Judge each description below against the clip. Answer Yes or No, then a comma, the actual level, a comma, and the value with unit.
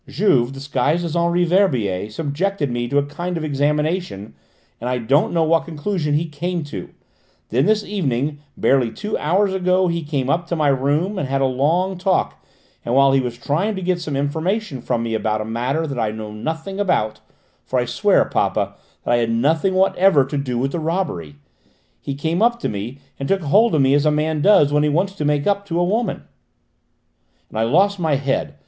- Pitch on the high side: No, medium, 150 Hz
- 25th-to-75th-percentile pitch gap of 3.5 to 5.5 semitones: Yes, average, 5.0 semitones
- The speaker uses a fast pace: Yes, fast, 210 wpm